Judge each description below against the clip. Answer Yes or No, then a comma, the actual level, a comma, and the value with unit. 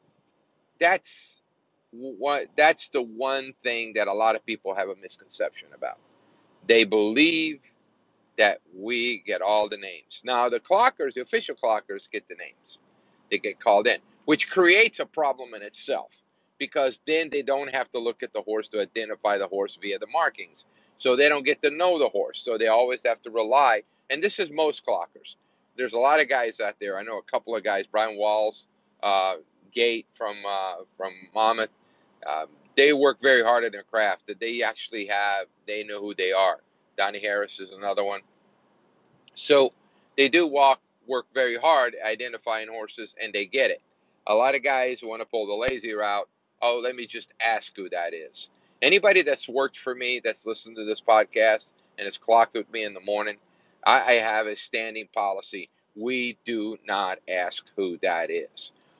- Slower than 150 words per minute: No, average, 185 wpm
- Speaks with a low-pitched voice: Yes, low, 125 Hz